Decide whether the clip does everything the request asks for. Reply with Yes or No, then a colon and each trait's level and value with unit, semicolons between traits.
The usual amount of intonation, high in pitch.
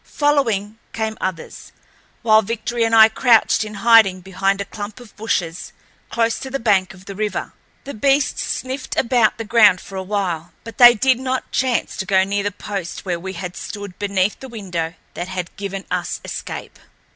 Yes: average, 3.5 semitones; high, 205 Hz